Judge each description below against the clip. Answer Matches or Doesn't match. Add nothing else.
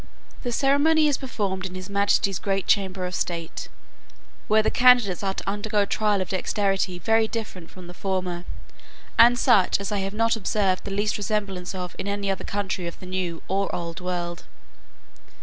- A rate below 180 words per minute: Doesn't match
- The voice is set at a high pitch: Matches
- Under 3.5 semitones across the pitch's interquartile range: Matches